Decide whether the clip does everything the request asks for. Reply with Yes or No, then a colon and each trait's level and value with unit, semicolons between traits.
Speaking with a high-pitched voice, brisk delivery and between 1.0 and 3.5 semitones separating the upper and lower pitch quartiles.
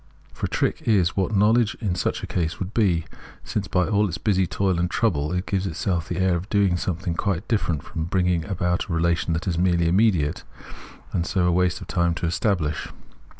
No: very low, 90 Hz; fast, 210 wpm; narrow, 2.6 semitones